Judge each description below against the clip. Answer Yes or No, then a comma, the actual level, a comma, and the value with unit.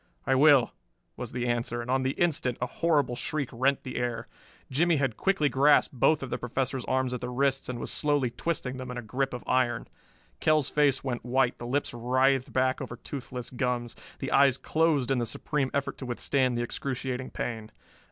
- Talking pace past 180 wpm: Yes, average, 200 wpm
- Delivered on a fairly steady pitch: Yes, narrow, 2.1 semitones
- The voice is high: No, low, 130 Hz